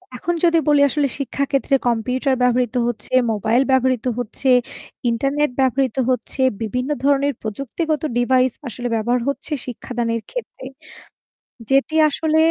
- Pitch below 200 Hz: No, very high, 260 Hz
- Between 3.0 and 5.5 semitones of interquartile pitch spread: No, narrow, 2.6 semitones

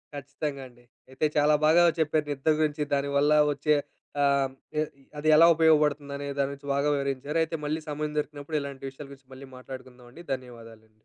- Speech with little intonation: Yes, narrow, 2.1 semitones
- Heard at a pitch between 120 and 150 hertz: Yes, medium, 140 Hz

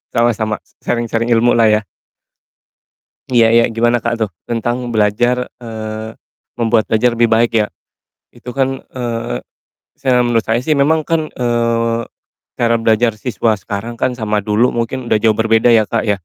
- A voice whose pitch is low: Yes, low, 115 Hz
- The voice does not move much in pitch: Yes, narrow, 1.6 semitones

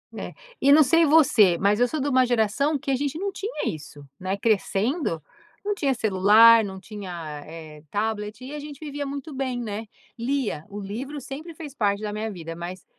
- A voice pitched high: Yes, high, 230 Hz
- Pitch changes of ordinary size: No, wide, 6.1 semitones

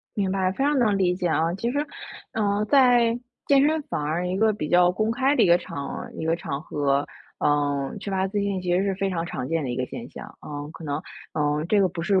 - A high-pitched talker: No, medium, 180 Hz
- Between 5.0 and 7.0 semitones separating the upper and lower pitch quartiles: Yes, wide, 5.5 semitones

